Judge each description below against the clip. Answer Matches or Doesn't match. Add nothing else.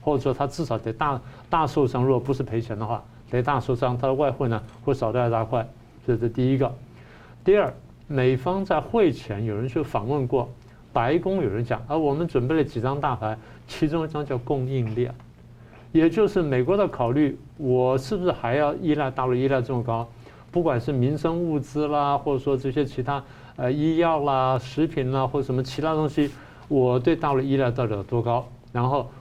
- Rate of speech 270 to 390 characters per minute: Matches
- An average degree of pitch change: Matches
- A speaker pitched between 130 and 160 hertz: Matches